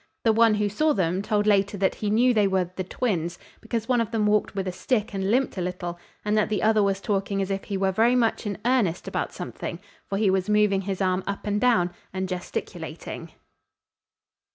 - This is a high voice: Yes, high, 200 Hz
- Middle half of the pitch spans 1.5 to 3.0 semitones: Yes, narrow, 2.5 semitones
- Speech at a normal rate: No, fast, 220 wpm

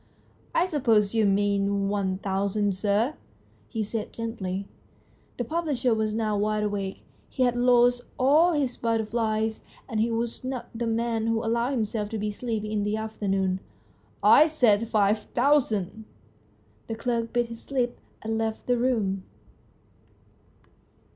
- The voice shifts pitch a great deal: No, average, 2.9 semitones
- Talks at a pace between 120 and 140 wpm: No, average, 155 wpm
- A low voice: No, high, 220 Hz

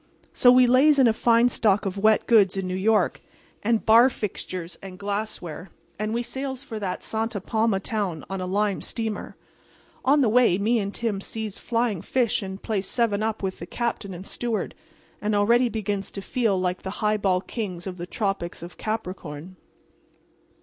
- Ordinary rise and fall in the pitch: Yes, average, 3.3 semitones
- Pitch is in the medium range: No, high, 210 Hz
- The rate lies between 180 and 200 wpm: Yes, average, 185 wpm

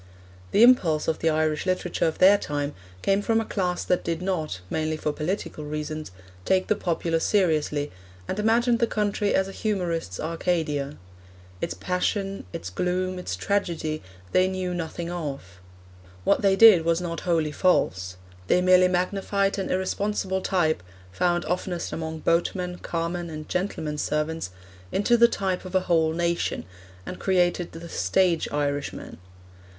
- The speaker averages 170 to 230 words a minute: No, average, 150 wpm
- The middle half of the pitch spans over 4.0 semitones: No, average, 3.3 semitones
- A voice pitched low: No, medium, 175 Hz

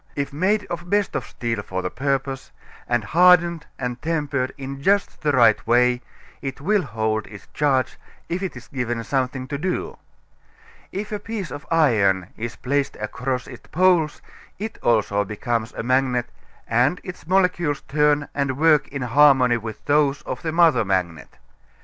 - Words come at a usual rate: Yes, average, 165 wpm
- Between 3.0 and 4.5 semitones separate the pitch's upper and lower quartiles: No, average, 5.3 semitones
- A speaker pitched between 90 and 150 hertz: Yes, low, 135 Hz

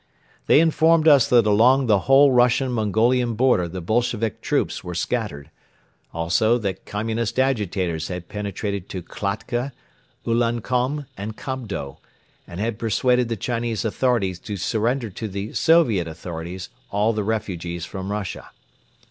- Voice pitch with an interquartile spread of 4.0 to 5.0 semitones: Yes, average, 4.3 semitones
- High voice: No, low, 110 Hz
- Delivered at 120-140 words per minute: Yes, slow, 135 wpm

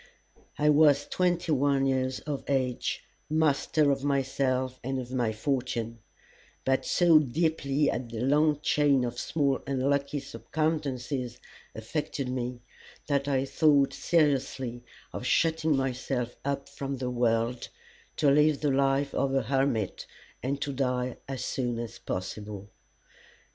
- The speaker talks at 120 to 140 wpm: Yes, slow, 135 wpm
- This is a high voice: No, low, 135 Hz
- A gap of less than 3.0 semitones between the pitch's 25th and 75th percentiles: Yes, narrow, 2.5 semitones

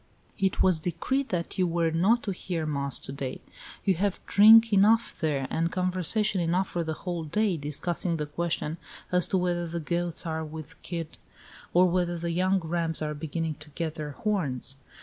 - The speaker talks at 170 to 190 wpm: Yes, average, 185 wpm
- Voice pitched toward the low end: No, medium, 170 Hz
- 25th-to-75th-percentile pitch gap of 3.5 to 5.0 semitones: No, average, 2.8 semitones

